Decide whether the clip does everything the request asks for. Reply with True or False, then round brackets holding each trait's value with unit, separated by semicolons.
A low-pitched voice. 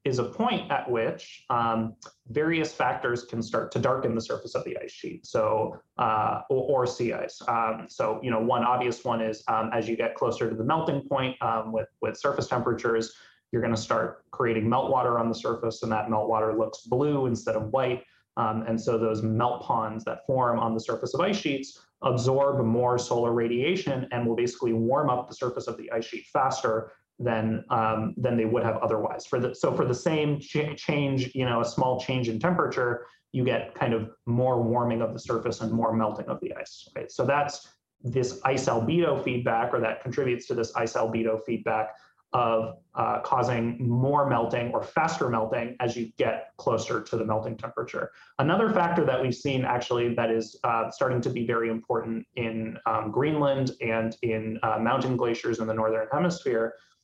True (120 Hz)